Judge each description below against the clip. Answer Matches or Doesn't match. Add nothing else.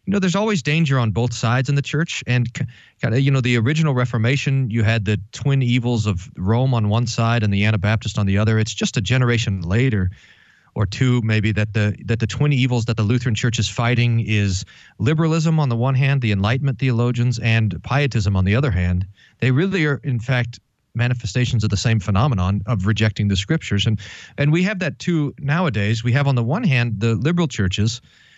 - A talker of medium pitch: Doesn't match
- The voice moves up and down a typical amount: Matches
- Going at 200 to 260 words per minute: Matches